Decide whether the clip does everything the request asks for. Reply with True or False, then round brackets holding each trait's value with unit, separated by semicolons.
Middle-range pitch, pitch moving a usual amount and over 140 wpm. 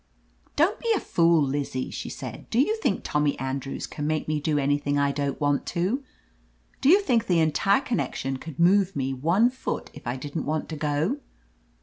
False (155 Hz; 5.9 semitones; 195 wpm)